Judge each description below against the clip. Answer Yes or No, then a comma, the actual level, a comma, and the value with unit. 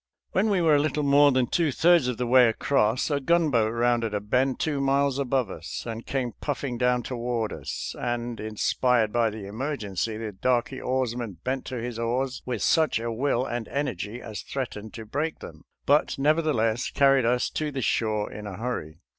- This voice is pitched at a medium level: No, low, 125 Hz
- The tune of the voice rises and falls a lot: No, average, 3.6 semitones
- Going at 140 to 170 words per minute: No, average, 190 wpm